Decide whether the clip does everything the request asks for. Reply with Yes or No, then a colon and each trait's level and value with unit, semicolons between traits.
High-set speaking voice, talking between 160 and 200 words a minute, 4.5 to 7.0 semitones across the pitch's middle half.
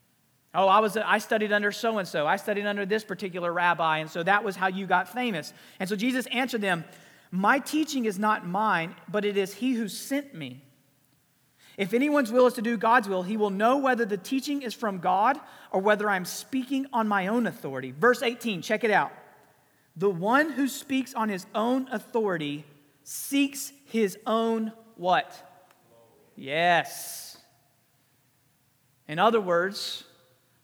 Yes: high, 205 Hz; average, 165 wpm; average, 5.2 semitones